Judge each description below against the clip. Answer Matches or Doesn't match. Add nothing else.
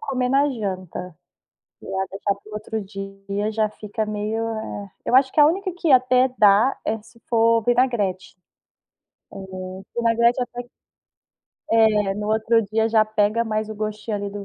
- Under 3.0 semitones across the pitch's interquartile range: Matches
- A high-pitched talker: Matches